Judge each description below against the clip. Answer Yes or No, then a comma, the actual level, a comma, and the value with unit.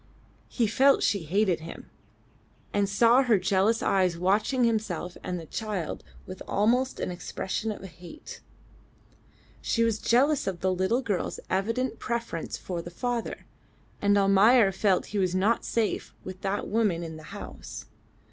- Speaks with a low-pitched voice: No, high, 200 Hz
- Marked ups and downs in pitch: No, average, 3.9 semitones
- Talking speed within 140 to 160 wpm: Yes, average, 150 wpm